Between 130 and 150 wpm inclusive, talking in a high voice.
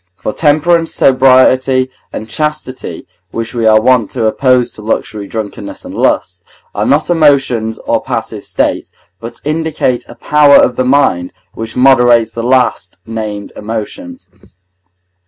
No: average, 140 wpm; low, 125 Hz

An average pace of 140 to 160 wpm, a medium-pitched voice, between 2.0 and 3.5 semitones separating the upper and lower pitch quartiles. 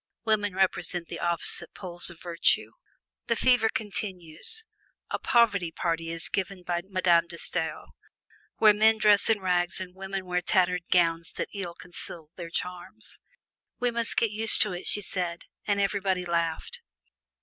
Yes: average, 155 wpm; medium, 180 Hz; average, 3.2 semitones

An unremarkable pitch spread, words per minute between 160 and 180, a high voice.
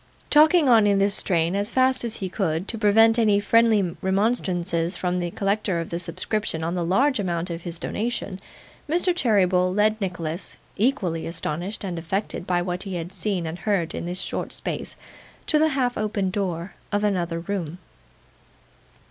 Yes: average, 3.8 semitones; average, 175 wpm; high, 195 Hz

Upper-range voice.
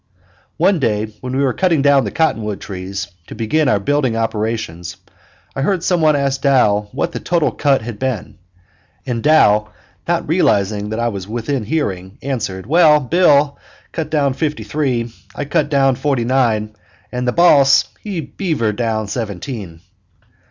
No: low, 130 Hz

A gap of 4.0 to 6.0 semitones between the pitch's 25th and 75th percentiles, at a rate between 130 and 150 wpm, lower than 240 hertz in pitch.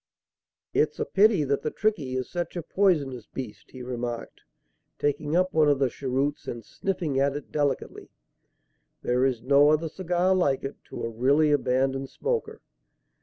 No: average, 4.3 semitones; average, 165 wpm; medium, 140 Hz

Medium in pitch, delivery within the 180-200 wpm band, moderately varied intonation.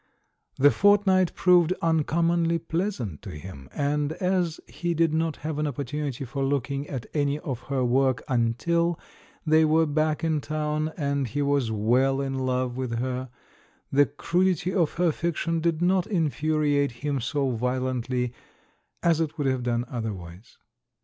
No: medium, 145 Hz; average, 150 wpm; average, 4.2 semitones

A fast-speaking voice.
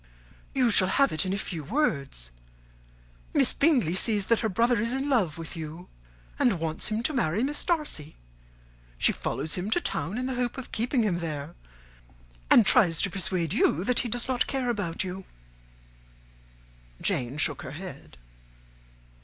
No: average, 170 wpm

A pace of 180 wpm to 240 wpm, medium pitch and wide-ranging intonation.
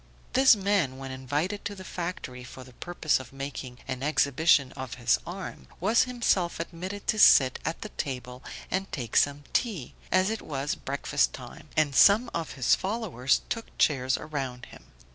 No: average, 170 wpm; medium, 150 Hz; wide, 6.4 semitones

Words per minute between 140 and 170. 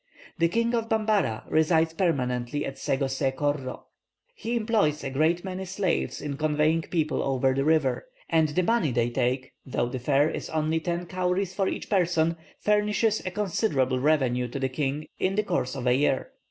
No: average, 180 wpm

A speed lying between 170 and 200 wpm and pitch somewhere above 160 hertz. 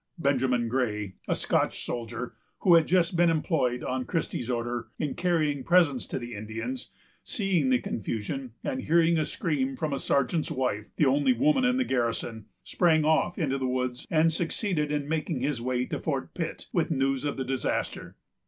No: average, 180 wpm; low, 135 Hz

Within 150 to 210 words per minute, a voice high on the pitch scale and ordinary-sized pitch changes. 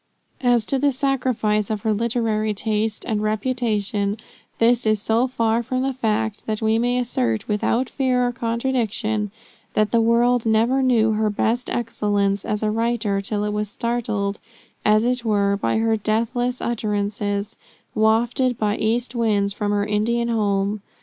No: average, 155 wpm; high, 220 Hz; narrow, 2.3 semitones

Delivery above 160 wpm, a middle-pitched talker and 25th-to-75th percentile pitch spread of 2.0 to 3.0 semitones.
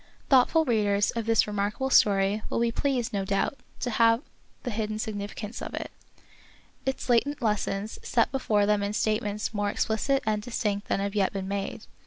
No: average, 175 wpm; high, 215 Hz; narrow, 2.6 semitones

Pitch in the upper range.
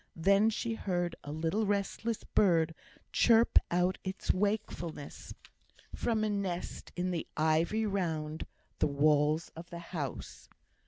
No: medium, 175 Hz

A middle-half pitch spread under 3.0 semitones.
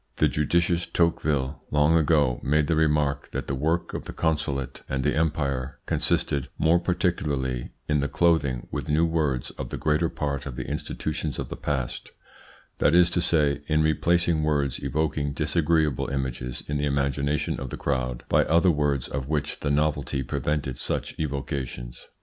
Yes: narrow, 2.6 semitones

